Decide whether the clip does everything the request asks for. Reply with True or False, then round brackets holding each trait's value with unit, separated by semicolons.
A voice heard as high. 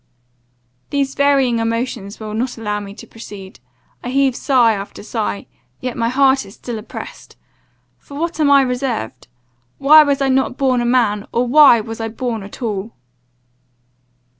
True (245 Hz)